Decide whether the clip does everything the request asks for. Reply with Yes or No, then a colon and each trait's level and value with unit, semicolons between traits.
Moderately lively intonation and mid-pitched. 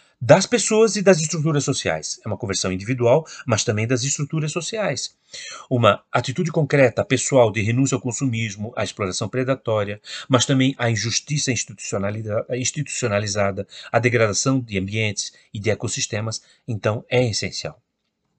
No: average, 4.4 semitones; low, 120 Hz